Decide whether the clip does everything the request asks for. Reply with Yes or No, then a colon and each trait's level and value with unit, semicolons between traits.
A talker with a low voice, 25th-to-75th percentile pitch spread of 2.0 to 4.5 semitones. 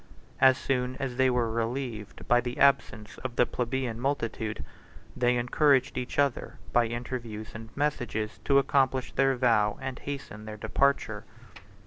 Yes: low, 125 Hz; average, 2.7 semitones